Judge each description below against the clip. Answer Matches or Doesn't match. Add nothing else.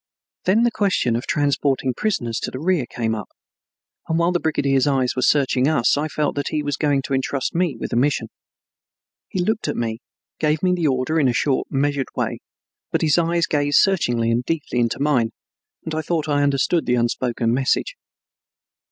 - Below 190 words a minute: Doesn't match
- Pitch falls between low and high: Matches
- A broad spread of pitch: Doesn't match